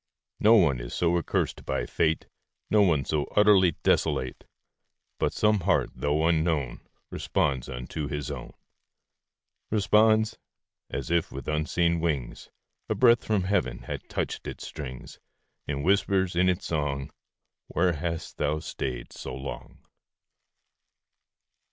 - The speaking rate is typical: No, slow, 120 wpm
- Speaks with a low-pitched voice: Yes, very low, 80 Hz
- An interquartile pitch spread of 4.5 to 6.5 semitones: Yes, average, 4.9 semitones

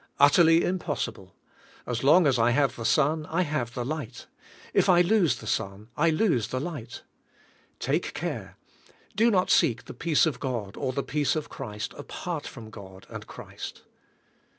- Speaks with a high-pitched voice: No, medium, 140 Hz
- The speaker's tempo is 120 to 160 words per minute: No, average, 170 wpm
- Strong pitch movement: Yes, wide, 5.7 semitones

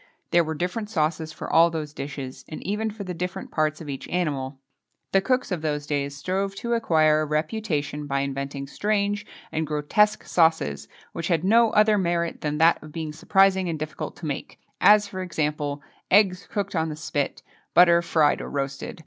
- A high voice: No, medium, 160 Hz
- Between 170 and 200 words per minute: Yes, average, 185 wpm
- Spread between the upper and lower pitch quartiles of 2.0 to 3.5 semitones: No, average, 4.5 semitones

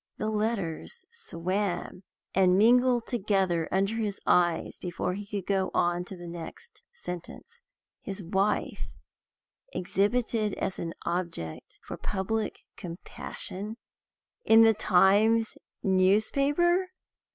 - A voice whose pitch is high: Yes, high, 200 Hz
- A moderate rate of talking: No, slow, 105 wpm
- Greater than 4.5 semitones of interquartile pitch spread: No, average, 3.8 semitones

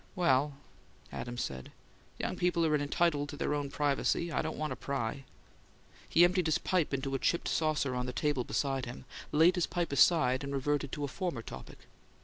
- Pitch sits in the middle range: Yes, medium, 145 Hz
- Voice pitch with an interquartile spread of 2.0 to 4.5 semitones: Yes, average, 3.4 semitones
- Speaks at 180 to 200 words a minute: Yes, average, 195 wpm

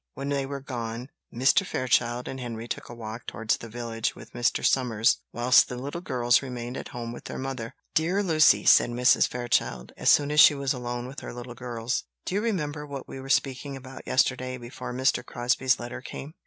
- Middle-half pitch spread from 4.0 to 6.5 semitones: No, narrow, 2.4 semitones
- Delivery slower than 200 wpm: No, fast, 205 wpm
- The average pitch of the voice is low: Yes, low, 125 Hz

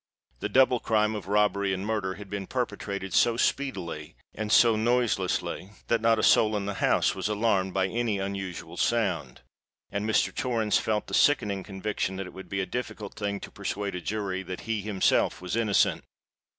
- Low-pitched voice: Yes, low, 100 Hz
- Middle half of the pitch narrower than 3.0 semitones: Yes, narrow, 2.5 semitones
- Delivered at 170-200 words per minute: Yes, average, 180 wpm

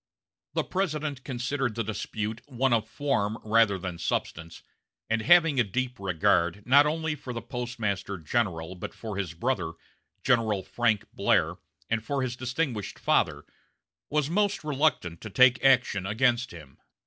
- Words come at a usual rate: Yes, average, 150 wpm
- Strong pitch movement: No, average, 4.9 semitones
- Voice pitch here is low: Yes, low, 120 Hz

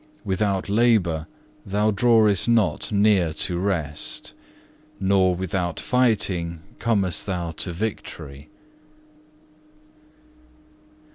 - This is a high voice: No, very low, 95 Hz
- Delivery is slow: Yes, slow, 80 wpm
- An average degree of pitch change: Yes, average, 3.7 semitones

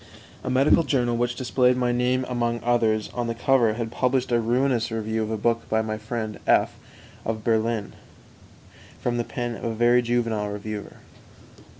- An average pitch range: No, narrow, 1.8 semitones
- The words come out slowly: No, average, 180 wpm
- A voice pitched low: Yes, low, 120 Hz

